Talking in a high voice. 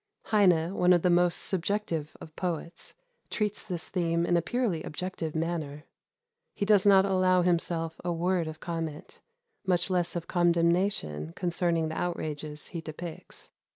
No: medium, 175 Hz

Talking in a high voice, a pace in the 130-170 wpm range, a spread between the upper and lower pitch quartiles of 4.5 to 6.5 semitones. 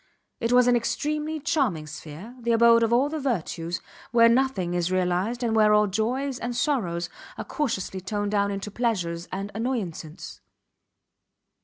Yes: high, 220 Hz; average, 155 wpm; average, 4.9 semitones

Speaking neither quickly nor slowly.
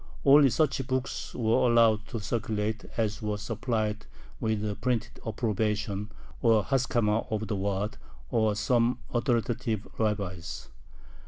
No: slow, 120 wpm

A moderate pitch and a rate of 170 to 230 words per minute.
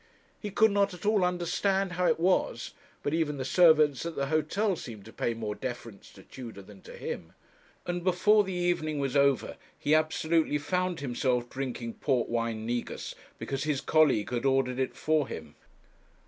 Yes: medium, 150 Hz; average, 175 wpm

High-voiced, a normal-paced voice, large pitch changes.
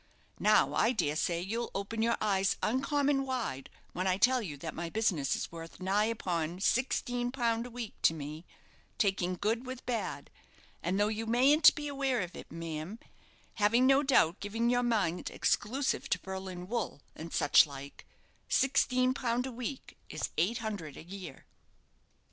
Yes: high, 215 Hz; average, 165 wpm; wide, 5.8 semitones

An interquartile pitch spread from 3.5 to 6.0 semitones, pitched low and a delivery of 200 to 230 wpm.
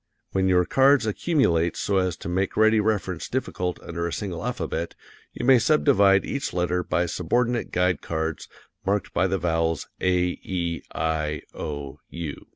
No: average, 4.1 semitones; very low, 90 Hz; average, 160 wpm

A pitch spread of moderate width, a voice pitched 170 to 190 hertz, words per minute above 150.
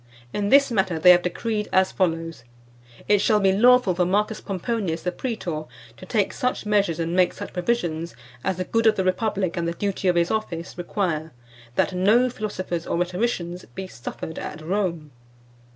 Yes: average, 3.6 semitones; medium, 185 Hz; average, 180 wpm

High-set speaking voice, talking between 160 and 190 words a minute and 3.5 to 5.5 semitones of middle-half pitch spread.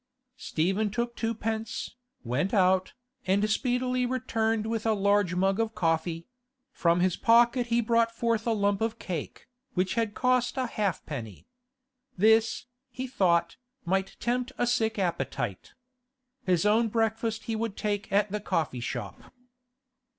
No: high, 215 Hz; average, 140 wpm; average, 3.9 semitones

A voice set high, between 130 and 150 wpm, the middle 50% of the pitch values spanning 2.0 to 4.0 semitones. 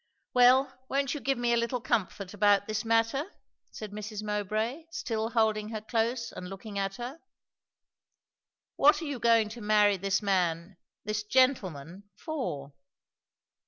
Yes: high, 220 Hz; average, 145 wpm; average, 3.3 semitones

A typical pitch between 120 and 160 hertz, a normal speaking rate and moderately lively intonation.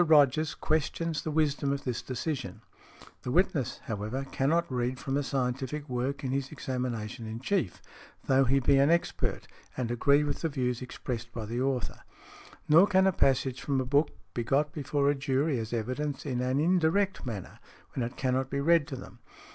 Yes: low, 135 Hz; average, 185 wpm; average, 3.1 semitones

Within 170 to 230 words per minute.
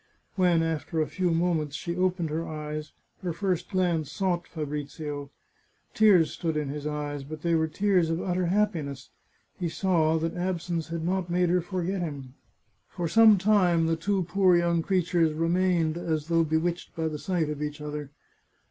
Yes: average, 175 wpm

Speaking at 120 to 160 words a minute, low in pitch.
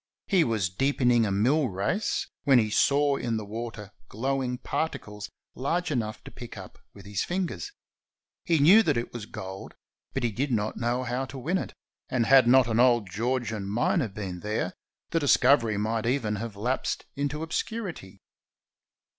No: average, 170 wpm; low, 120 Hz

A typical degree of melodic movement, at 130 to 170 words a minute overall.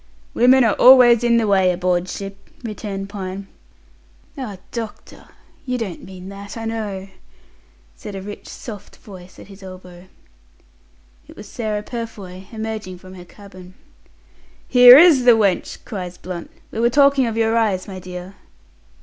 Yes: average, 3.6 semitones; average, 150 wpm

